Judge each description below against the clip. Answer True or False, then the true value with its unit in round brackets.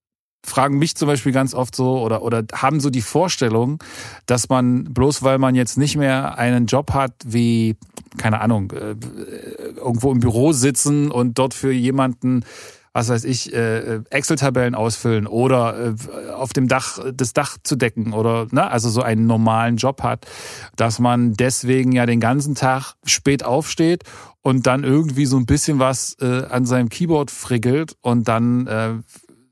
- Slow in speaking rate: False (160 wpm)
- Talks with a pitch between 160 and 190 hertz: False (125 Hz)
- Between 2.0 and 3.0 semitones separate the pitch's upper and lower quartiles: True (2.5 semitones)